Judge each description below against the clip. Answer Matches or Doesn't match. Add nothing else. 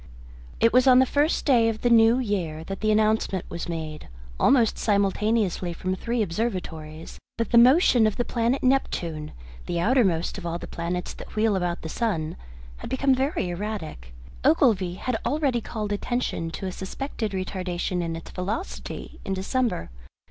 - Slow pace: Doesn't match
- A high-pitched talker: Matches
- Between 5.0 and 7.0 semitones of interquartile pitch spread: Matches